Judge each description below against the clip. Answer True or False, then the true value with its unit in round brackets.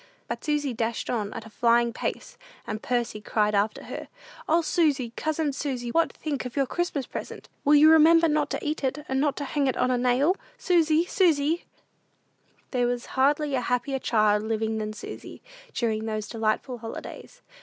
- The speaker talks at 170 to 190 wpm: True (180 wpm)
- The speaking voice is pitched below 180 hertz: False (260 Hz)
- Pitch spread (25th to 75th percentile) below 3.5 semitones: False (4.9 semitones)